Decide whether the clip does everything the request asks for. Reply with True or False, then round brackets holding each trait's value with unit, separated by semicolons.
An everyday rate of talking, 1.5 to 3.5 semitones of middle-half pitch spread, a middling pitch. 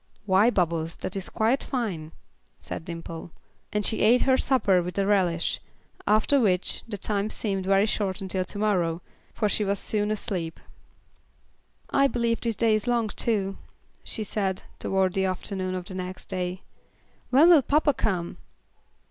False (160 wpm; 3.1 semitones; 200 Hz)